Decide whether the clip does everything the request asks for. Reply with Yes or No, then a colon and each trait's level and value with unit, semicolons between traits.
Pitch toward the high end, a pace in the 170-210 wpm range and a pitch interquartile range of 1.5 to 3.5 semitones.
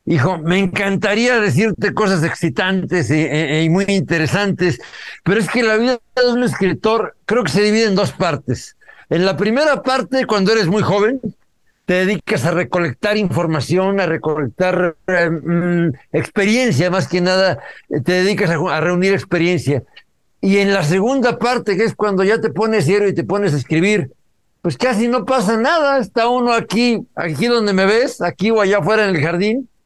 No: high, 195 Hz; average, 175 wpm; average, 4.2 semitones